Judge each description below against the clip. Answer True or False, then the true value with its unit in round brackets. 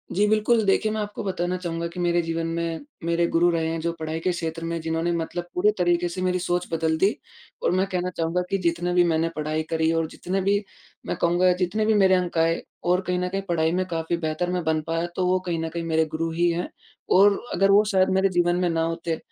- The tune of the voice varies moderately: False (1.9 semitones)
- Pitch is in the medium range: True (175 Hz)